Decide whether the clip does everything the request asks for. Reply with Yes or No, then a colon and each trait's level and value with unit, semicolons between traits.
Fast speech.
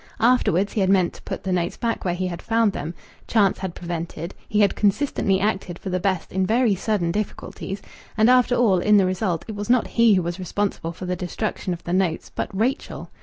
Yes: fast, 220 wpm